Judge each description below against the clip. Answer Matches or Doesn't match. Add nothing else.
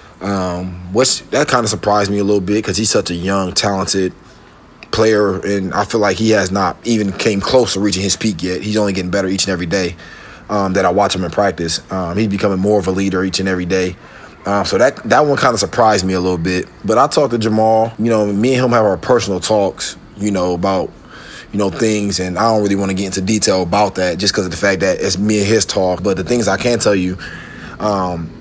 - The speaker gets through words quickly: Matches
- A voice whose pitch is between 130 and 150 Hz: Doesn't match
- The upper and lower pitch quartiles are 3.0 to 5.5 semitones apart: Doesn't match